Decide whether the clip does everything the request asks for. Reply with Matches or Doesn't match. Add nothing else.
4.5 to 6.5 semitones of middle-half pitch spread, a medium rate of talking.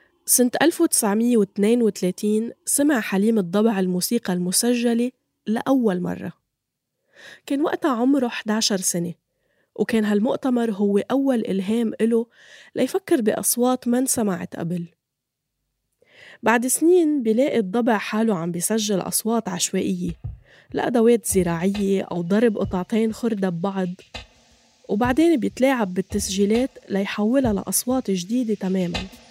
Doesn't match